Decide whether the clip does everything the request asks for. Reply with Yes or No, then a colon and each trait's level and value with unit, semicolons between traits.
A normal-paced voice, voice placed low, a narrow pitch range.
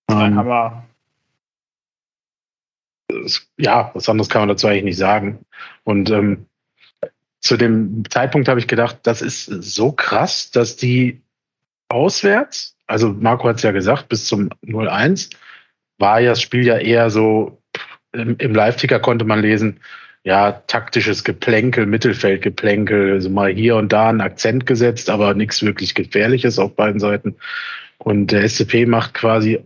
Yes: average, 145 wpm; low, 110 Hz; narrow, 2.3 semitones